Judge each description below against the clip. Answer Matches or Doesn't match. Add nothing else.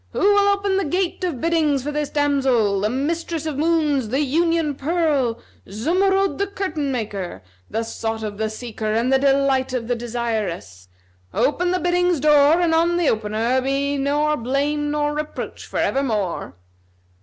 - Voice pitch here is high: Matches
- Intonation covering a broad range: Matches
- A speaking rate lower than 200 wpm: Matches